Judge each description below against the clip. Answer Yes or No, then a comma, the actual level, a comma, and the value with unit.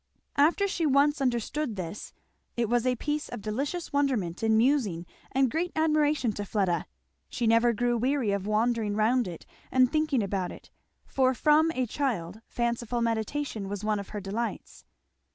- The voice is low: No, high, 235 Hz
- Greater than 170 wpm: No, average, 165 wpm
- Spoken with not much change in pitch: No, average, 5.1 semitones